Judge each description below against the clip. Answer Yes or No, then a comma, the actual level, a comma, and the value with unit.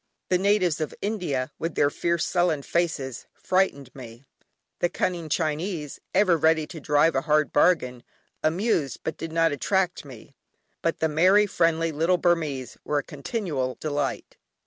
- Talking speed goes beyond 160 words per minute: No, average, 150 wpm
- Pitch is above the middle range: No, medium, 160 Hz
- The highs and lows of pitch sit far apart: No, average, 3.4 semitones